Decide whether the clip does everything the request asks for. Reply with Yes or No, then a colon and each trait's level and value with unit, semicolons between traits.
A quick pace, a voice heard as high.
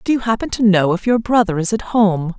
Yes: fast, 275 wpm; high, 205 Hz